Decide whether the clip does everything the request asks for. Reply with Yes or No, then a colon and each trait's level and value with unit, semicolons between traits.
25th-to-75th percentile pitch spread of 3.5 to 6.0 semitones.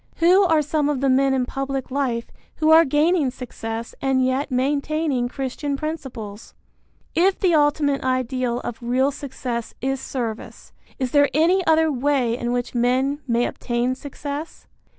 No: average, 3.0 semitones